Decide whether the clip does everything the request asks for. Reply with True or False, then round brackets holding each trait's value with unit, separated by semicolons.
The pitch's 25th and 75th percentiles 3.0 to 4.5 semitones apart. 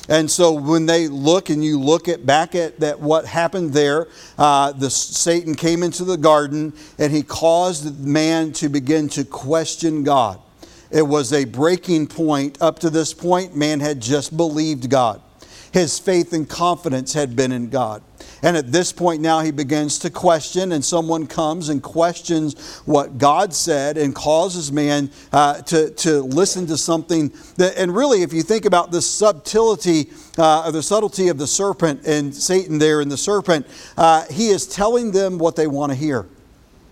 False (2.5 semitones)